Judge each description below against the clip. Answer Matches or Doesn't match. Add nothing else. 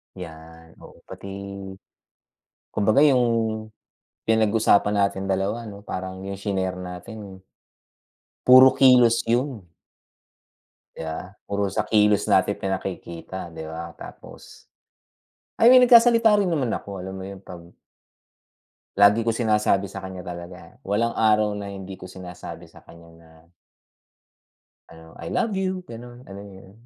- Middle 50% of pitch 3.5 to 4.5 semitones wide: Matches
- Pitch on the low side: Matches